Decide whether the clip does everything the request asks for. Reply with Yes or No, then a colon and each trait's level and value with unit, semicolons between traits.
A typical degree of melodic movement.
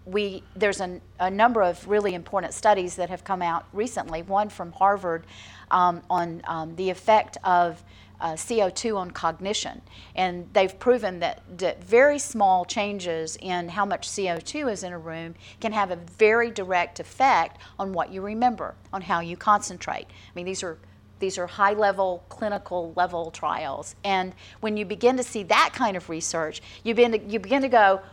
Yes: average, 3.3 semitones